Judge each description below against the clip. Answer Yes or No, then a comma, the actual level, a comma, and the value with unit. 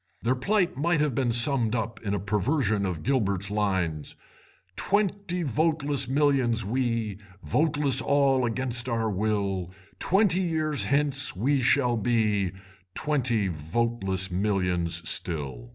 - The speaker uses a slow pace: Yes, slow, 120 wpm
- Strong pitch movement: Yes, wide, 6.2 semitones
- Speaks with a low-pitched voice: Yes, low, 120 Hz